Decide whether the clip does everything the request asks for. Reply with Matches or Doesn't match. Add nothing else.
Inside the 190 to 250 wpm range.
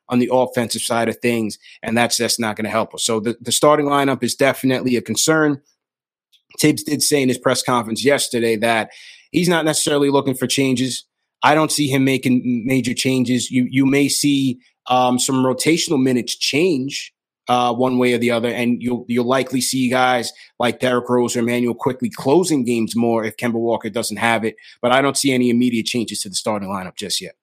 Matches